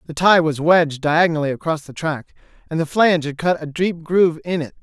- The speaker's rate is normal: No, fast, 225 wpm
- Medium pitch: Yes, medium, 160 Hz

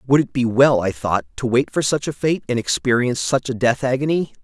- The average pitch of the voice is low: Yes, low, 130 Hz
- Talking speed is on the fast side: Yes, fast, 245 wpm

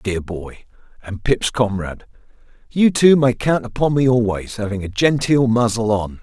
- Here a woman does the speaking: No, male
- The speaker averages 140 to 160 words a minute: No, average, 175 wpm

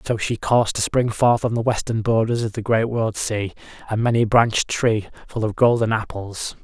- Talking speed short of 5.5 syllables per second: Yes, 5.1 syllables/s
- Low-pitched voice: Yes, low, 110 Hz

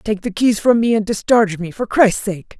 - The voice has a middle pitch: No, high, 210 Hz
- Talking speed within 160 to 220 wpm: No, fast, 255 wpm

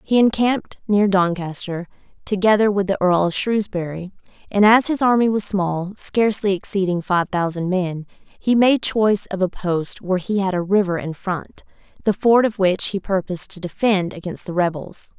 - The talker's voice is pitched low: No, high, 195 Hz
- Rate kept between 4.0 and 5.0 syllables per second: Yes, 4.9 syllables/s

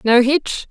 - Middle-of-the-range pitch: No, very high, 260 Hz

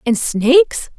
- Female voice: Yes, female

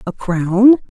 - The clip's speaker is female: Yes, female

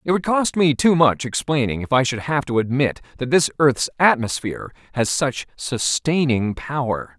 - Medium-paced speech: Yes, average, 175 wpm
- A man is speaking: Yes, male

